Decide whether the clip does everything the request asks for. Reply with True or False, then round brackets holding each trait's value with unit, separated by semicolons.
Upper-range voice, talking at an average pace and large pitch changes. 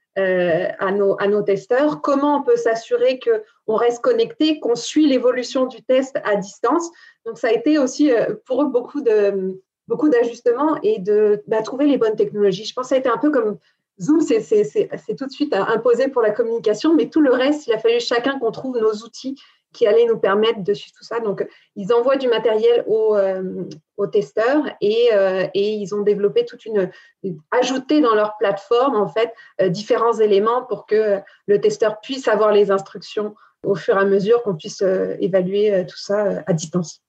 False (230 Hz; 205 wpm; 4.9 semitones)